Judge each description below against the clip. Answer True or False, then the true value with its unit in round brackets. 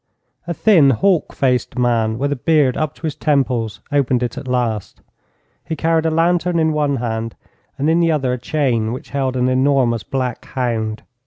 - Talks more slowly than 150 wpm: False (185 wpm)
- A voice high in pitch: False (135 Hz)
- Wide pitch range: False (4.2 semitones)